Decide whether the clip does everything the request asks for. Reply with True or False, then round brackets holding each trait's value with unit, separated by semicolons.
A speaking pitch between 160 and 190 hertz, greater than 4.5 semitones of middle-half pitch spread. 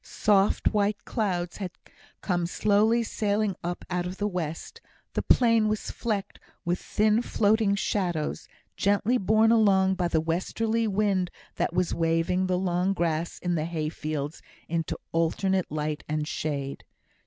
False (185 Hz; 3.9 semitones)